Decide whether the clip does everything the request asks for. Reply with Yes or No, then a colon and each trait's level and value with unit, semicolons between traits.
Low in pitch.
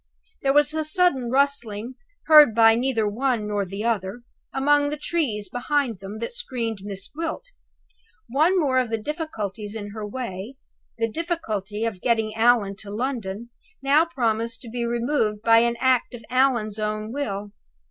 No: high, 235 Hz